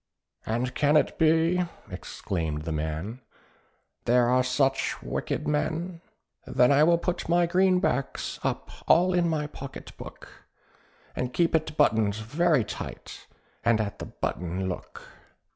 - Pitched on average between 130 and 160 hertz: Yes, medium, 140 Hz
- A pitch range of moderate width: No, wide, 7.1 semitones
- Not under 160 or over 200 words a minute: No, slow, 135 wpm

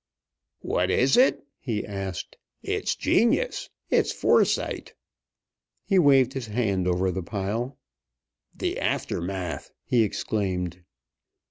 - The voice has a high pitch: No, low, 105 Hz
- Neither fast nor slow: No, slow, 105 wpm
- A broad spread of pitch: Yes, wide, 5.8 semitones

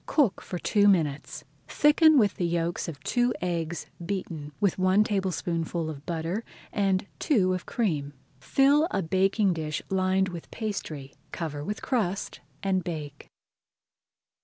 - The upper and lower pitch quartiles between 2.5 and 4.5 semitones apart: Yes, average, 3.8 semitones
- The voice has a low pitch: No, medium, 185 Hz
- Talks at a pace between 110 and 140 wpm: Yes, slow, 135 wpm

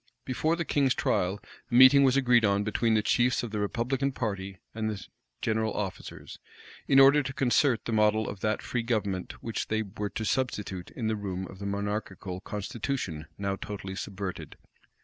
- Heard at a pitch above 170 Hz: No, low, 110 Hz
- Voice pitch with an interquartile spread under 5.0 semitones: Yes, average, 3.8 semitones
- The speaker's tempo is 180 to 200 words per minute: Yes, average, 185 wpm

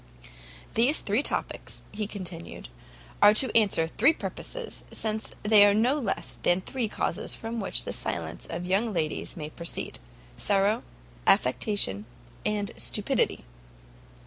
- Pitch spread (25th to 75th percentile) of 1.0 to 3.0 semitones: No, average, 3.9 semitones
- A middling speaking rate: No, slow, 130 wpm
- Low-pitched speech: No, high, 210 Hz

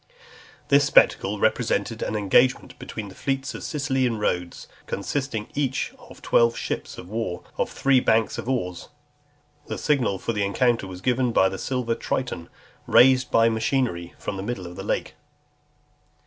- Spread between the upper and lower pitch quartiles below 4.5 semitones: No, average, 4.9 semitones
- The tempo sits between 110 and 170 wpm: Yes, average, 160 wpm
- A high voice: No, low, 115 Hz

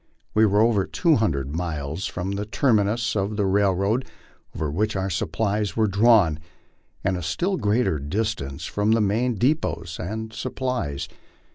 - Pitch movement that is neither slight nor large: Yes, average, 4.1 semitones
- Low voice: Yes, low, 105 Hz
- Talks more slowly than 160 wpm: Yes, average, 150 wpm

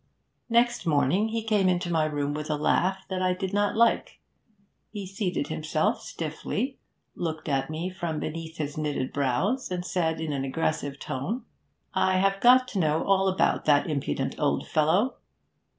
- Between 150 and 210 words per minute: Yes, average, 165 wpm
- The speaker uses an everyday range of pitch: Yes, average, 4.4 semitones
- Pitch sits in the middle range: Yes, medium, 175 Hz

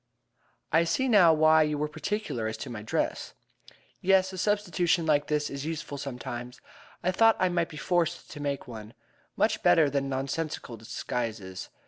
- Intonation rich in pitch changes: Yes, wide, 5.7 semitones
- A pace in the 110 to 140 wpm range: No, average, 165 wpm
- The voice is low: No, medium, 150 Hz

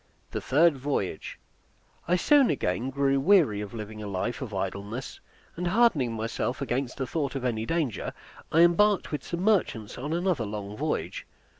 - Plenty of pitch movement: Yes, wide, 7.5 semitones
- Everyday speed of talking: Yes, average, 165 wpm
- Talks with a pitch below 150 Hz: Yes, low, 135 Hz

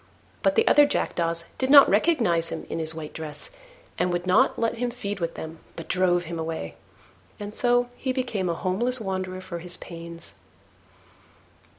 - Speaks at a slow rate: No, average, 175 wpm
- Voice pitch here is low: No, medium, 185 Hz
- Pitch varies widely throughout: Yes, wide, 6.2 semitones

